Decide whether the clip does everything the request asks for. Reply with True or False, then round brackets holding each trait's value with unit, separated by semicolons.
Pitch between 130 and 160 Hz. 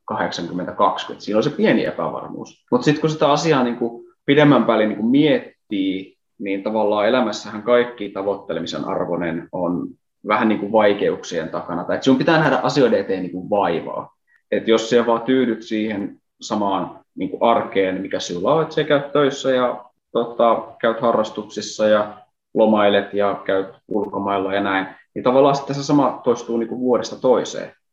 False (110 Hz)